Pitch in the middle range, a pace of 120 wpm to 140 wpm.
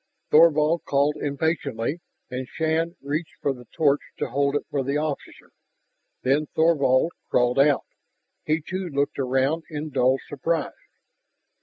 Yes: medium, 145 Hz; slow, 135 wpm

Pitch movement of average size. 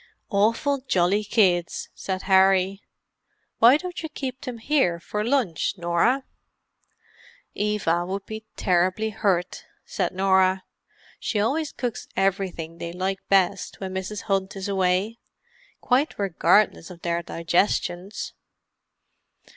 Yes: average, 3.4 semitones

